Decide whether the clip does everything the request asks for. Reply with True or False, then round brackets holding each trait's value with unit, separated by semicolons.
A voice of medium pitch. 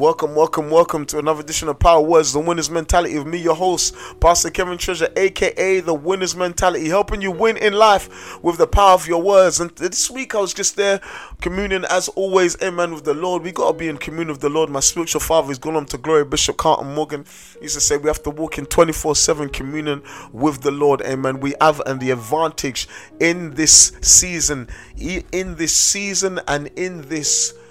True (165 Hz)